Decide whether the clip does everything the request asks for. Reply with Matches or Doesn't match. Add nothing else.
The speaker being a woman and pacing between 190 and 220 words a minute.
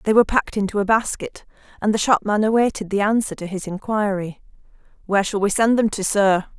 Matches